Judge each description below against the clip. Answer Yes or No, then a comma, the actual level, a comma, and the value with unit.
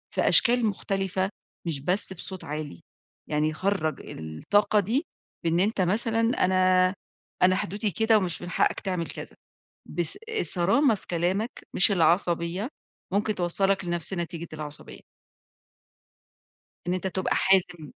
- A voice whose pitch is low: No, medium, 185 Hz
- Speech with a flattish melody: No, average, 3.0 semitones